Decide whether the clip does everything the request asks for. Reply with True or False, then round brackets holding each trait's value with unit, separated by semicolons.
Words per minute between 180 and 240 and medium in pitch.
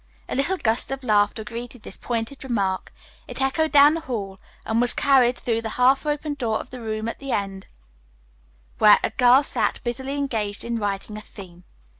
False (190 wpm; 240 Hz)